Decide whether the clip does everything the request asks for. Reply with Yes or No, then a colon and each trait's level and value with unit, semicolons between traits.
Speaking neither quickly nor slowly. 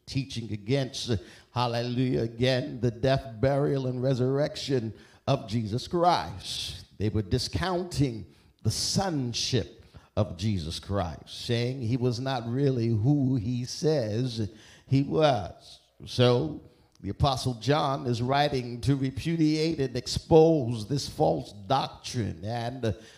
No: slow, 115 wpm